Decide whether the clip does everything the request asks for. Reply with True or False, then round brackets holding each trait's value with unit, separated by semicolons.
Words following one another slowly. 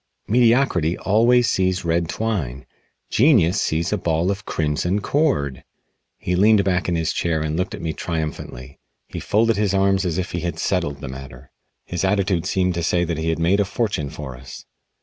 False (190 wpm)